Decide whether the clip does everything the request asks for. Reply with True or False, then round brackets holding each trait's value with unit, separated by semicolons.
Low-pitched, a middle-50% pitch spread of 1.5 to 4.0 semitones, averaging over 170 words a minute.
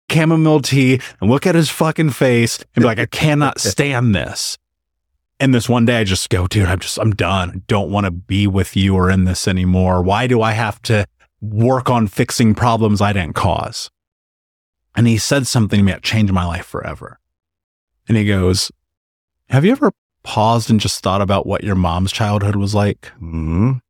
False (100 Hz; 4.5 semitones; 200 wpm)